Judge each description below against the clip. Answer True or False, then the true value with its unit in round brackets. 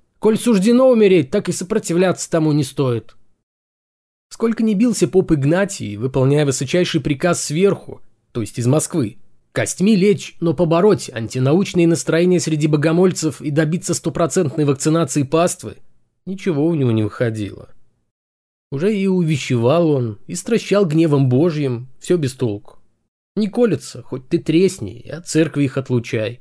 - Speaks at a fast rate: False (140 wpm)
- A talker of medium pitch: True (160 Hz)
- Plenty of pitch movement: True (5.7 semitones)